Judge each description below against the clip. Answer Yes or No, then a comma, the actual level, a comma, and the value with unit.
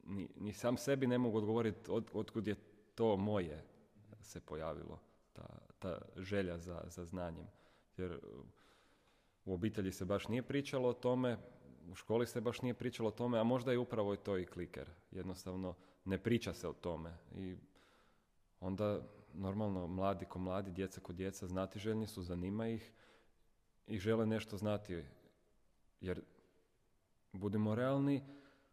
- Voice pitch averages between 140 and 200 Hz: No, low, 100 Hz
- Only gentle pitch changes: No, average, 3.7 semitones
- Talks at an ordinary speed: Yes, average, 150 wpm